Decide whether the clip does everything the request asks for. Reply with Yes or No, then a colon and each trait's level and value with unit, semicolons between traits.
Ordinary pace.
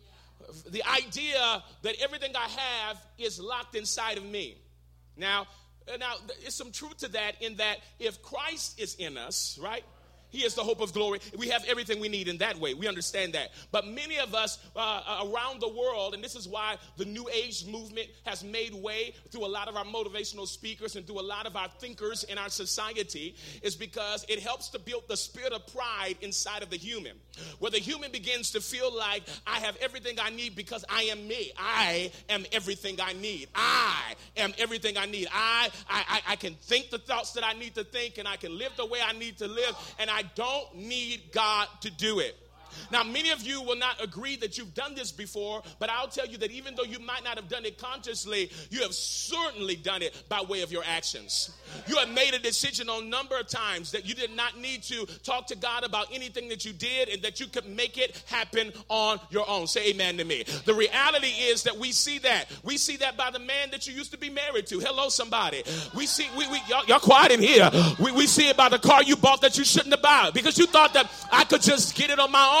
No: fast, 230 wpm